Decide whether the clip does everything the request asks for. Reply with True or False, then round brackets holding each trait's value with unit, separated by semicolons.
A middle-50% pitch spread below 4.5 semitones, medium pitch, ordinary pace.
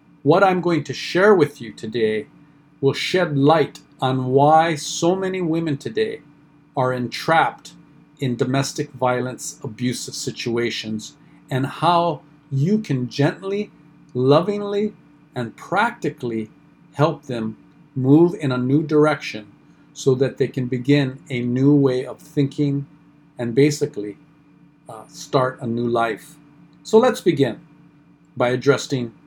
False (3.2 semitones; 145 Hz; 125 wpm)